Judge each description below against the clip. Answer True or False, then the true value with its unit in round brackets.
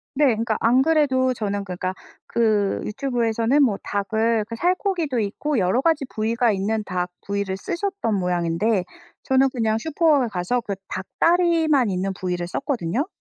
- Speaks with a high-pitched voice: True (225 Hz)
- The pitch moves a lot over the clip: True (5.7 semitones)